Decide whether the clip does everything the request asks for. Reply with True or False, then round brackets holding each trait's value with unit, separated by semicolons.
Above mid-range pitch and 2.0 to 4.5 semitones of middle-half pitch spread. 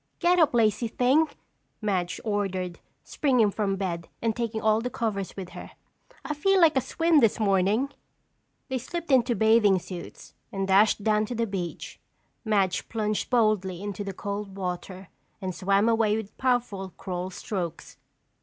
True (210 Hz; 3.5 semitones)